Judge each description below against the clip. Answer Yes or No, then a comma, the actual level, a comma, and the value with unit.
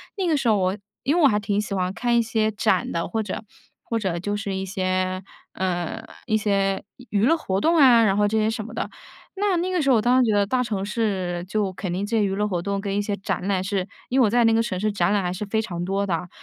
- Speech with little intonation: No, average, 3.1 semitones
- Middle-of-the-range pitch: No, high, 205 Hz